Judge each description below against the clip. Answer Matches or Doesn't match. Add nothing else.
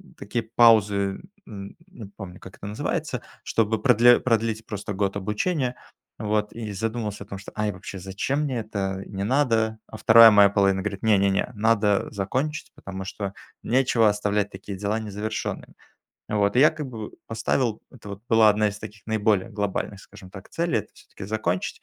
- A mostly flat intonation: Matches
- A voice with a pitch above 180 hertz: Doesn't match